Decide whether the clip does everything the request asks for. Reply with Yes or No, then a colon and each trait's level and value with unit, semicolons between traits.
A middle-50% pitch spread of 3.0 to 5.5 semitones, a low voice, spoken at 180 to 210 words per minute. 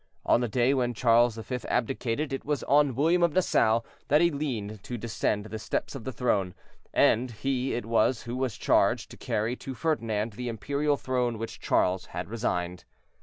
Yes: average, 3.6 semitones; low, 120 Hz; average, 185 wpm